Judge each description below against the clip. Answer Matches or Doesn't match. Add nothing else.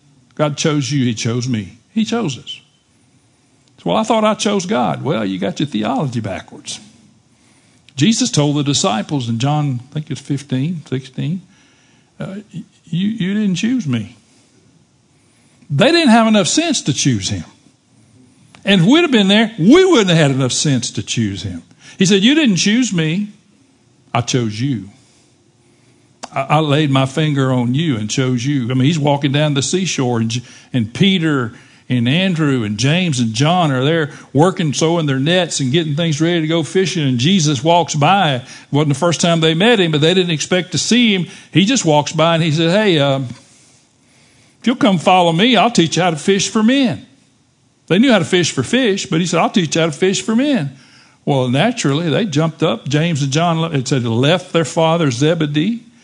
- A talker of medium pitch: Matches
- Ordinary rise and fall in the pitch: Doesn't match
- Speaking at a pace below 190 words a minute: Doesn't match